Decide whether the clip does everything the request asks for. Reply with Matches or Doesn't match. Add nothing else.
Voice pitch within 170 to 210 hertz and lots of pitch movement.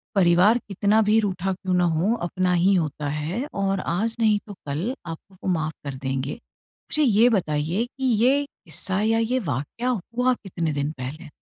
Matches